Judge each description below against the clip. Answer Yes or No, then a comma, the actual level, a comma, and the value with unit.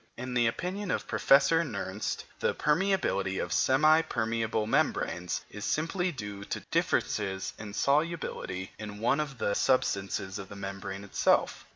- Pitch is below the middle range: Yes, low, 115 Hz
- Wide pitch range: Yes, wide, 7.2 semitones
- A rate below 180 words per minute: Yes, average, 145 wpm